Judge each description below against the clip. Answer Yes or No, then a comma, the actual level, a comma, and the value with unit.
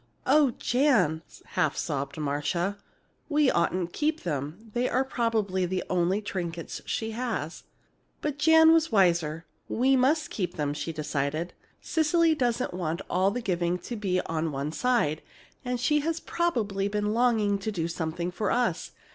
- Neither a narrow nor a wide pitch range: No, wide, 6.8 semitones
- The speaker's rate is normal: Yes, average, 155 wpm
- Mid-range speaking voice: No, high, 200 Hz